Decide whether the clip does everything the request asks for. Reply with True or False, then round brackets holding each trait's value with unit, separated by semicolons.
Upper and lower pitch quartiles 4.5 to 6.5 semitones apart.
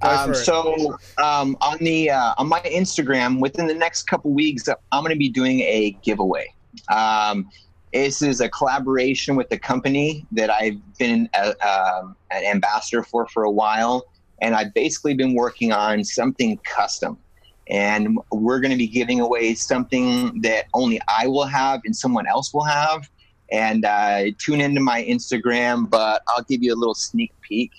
True (5.5 semitones)